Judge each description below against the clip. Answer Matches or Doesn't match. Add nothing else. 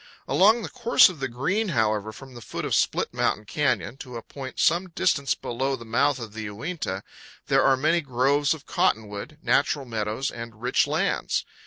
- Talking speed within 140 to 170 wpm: Doesn't match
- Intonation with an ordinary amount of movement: Matches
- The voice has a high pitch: Doesn't match